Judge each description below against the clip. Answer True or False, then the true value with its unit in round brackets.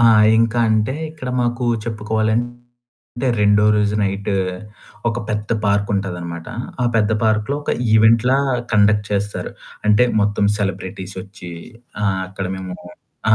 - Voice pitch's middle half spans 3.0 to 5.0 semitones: False (2.4 semitones)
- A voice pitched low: True (105 Hz)